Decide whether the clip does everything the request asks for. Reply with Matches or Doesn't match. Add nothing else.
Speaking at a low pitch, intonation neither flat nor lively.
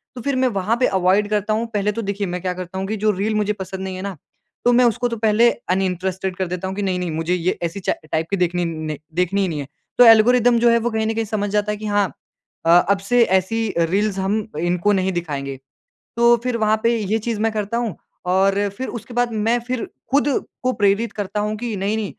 Doesn't match